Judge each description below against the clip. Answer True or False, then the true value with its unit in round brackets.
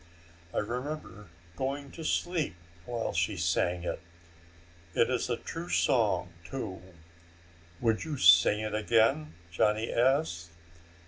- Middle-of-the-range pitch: False (115 Hz)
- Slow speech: True (120 wpm)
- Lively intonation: True (6.3 semitones)